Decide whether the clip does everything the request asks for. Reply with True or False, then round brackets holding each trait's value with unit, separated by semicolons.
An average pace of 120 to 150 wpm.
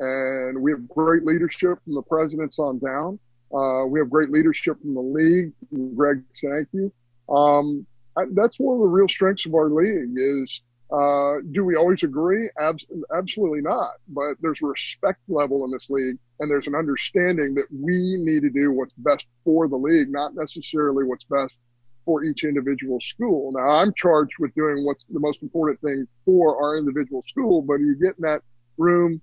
False (185 wpm)